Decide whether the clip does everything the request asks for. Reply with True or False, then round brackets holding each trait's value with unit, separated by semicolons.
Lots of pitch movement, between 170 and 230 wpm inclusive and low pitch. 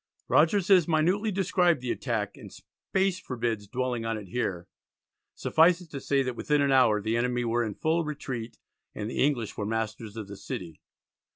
True (6.1 semitones; 185 wpm; 125 Hz)